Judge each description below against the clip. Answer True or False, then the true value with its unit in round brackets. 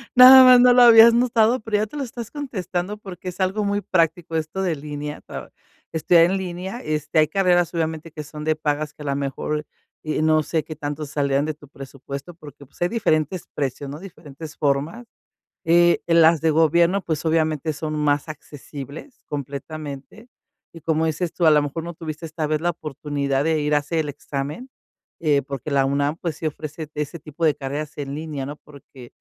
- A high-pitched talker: False (155 Hz)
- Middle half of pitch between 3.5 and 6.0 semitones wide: False (3.1 semitones)